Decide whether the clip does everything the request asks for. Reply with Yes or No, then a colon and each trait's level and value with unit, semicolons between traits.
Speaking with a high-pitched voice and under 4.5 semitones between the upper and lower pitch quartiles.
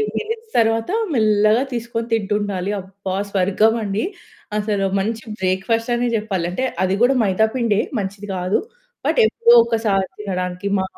Yes: high, 210 Hz; average, 2.9 semitones